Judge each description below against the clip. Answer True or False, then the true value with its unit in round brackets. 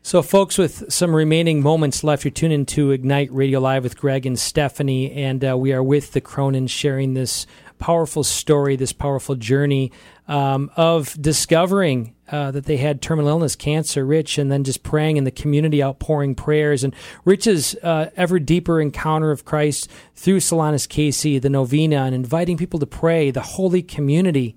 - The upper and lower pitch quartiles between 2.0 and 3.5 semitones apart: True (2.7 semitones)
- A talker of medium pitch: True (145 Hz)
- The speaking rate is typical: True (180 wpm)